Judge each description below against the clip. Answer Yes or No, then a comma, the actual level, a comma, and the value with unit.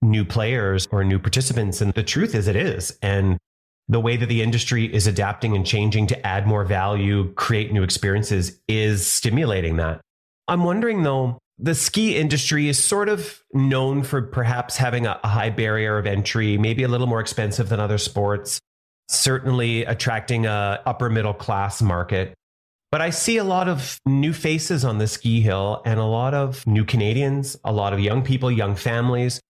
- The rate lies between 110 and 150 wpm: No, average, 180 wpm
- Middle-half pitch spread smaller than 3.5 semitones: No, average, 4.0 semitones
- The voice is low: Yes, low, 115 Hz